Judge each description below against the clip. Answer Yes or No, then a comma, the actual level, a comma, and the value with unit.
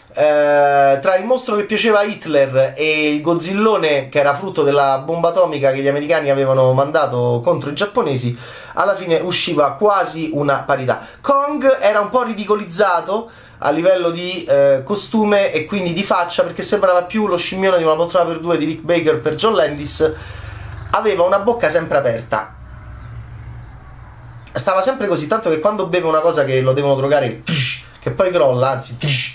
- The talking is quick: Yes, fast, 175 wpm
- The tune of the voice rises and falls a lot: Yes, wide, 6.2 semitones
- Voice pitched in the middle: Yes, medium, 160 Hz